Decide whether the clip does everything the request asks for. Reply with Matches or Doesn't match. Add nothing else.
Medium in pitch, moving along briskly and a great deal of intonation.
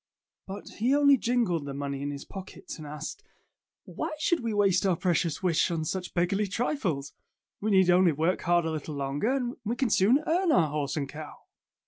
Doesn't match